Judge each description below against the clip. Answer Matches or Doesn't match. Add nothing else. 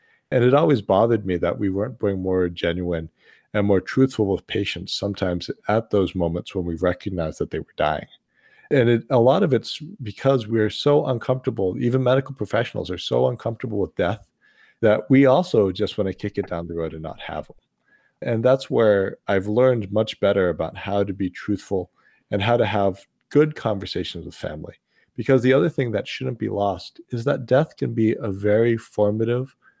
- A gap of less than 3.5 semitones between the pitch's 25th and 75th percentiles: Doesn't match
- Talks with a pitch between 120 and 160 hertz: Doesn't match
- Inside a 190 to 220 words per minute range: Matches